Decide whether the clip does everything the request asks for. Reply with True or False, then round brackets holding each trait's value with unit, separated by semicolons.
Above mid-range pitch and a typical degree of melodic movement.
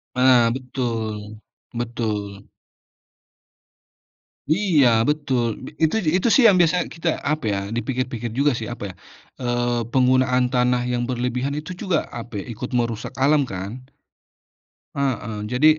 False (125 Hz; 3.3 semitones)